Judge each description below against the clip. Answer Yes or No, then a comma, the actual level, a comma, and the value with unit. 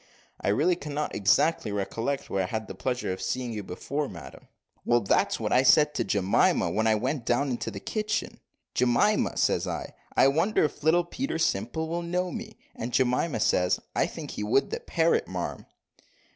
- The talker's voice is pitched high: No, low, 130 Hz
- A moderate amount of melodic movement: No, wide, 7.4 semitones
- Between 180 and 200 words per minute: Yes, average, 185 wpm